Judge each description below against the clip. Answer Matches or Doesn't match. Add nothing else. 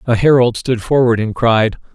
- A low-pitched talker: Matches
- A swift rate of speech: Doesn't match